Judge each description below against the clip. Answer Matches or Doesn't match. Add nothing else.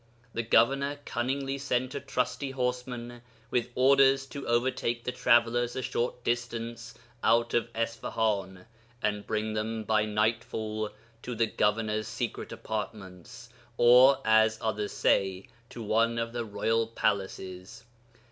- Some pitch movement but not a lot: Doesn't match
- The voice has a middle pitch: Doesn't match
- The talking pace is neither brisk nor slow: Doesn't match